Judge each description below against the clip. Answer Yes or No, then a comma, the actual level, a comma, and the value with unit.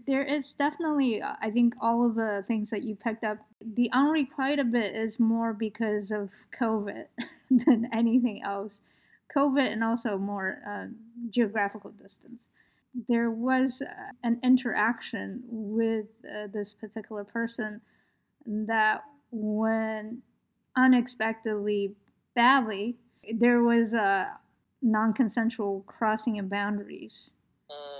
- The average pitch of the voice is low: No, high, 230 Hz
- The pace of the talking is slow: Yes, slow, 115 wpm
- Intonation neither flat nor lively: No, narrow, 2.3 semitones